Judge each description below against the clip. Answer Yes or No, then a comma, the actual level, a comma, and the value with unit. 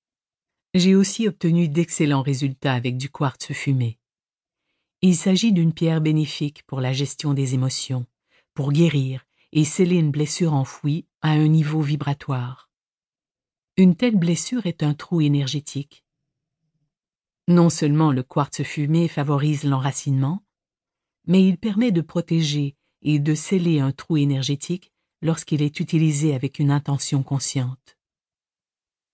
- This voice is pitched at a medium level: Yes, medium, 150 Hz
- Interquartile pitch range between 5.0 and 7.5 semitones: No, average, 3.2 semitones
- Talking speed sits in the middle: No, slow, 130 wpm